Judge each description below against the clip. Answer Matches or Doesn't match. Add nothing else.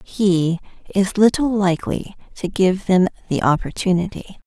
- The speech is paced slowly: Matches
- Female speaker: Matches